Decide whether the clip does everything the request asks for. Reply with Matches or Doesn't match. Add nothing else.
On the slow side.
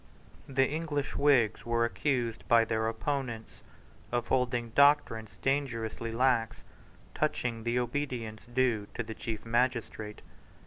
Matches